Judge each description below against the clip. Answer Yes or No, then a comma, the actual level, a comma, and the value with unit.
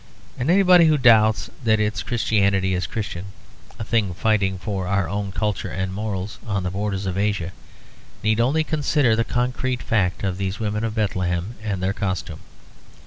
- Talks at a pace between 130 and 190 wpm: Yes, average, 170 wpm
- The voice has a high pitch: No, low, 105 Hz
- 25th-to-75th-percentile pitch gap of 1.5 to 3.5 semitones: Yes, average, 3.0 semitones